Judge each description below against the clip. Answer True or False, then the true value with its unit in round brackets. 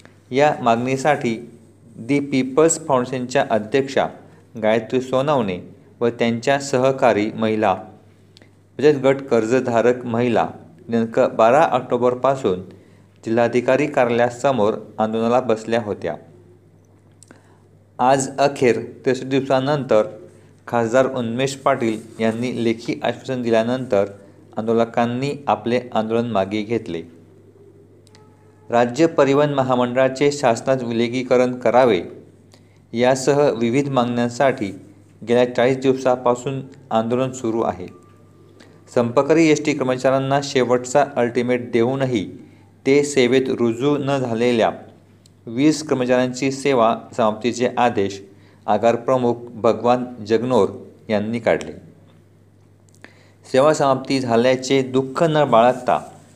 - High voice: False (120 Hz)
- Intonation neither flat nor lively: True (3.4 semitones)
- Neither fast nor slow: True (90 wpm)